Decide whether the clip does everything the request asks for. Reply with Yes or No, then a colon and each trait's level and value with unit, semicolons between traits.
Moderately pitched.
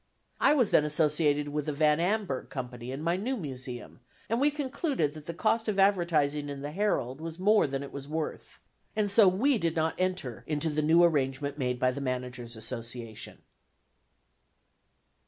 Yes: medium, 150 Hz